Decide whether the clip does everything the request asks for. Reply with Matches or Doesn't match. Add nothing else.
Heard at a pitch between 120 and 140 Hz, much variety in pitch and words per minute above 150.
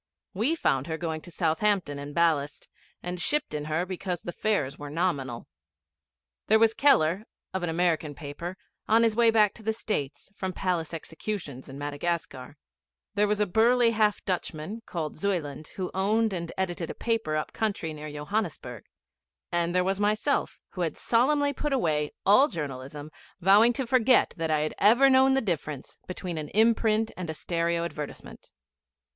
Doesn't match